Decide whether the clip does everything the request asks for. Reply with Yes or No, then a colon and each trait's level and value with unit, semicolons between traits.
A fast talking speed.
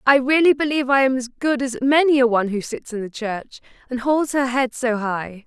Yes: fast, 240 wpm